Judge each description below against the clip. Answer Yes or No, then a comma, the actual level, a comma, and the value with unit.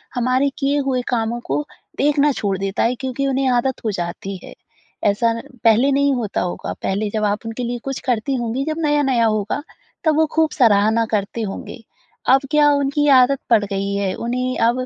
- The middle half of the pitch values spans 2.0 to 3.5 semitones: No, average, 4.3 semitones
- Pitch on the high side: Yes, high, 245 Hz